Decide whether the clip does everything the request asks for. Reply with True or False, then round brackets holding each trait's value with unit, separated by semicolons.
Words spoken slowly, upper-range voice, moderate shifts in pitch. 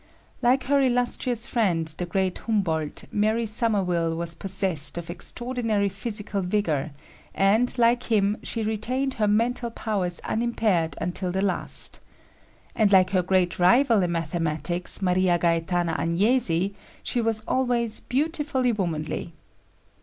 True (125 wpm; 200 Hz; 5.0 semitones)